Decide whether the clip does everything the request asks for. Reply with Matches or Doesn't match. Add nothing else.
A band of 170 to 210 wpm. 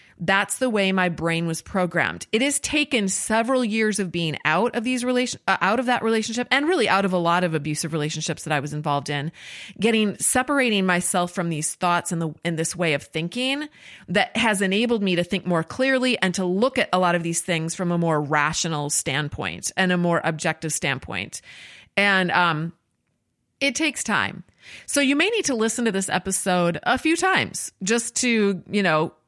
Matches